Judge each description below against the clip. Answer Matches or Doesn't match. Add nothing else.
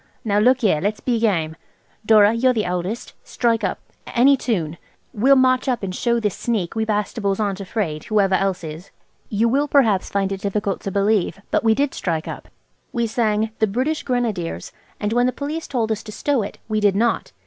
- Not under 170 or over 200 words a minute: Matches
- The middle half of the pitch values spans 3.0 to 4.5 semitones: Matches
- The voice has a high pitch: Matches